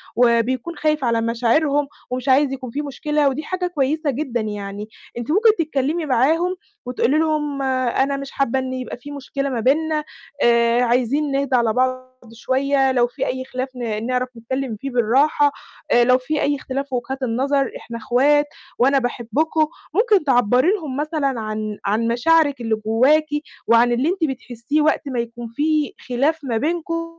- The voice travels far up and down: No, average, 3.7 semitones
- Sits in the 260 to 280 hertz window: Yes, very high, 265 Hz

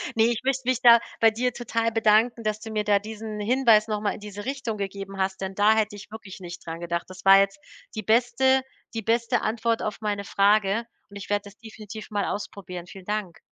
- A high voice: Yes, high, 215 Hz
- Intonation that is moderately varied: No, narrow, 2.3 semitones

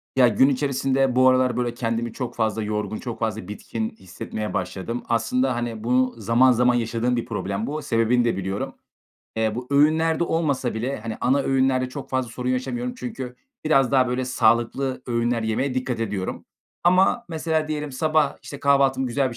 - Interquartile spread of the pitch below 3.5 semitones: Yes, average, 3.0 semitones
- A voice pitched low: Yes, low, 125 Hz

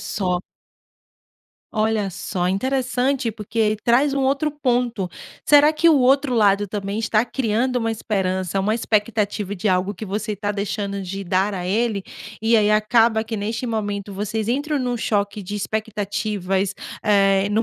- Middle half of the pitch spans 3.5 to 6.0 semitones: No, average, 3.0 semitones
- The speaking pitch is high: Yes, high, 215 Hz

